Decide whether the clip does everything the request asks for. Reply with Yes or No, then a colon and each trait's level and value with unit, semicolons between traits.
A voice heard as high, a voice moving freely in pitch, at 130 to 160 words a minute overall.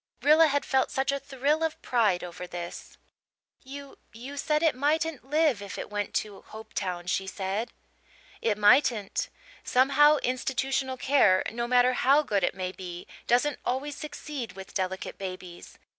Yes: very high, 250 Hz; wide, 6.4 semitones; average, 155 wpm